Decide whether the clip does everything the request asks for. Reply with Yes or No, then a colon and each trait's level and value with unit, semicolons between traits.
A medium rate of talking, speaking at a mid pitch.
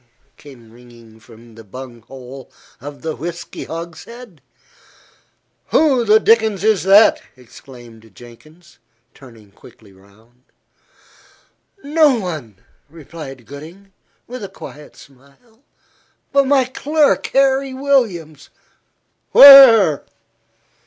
No: slow, 95 wpm; medium, 155 Hz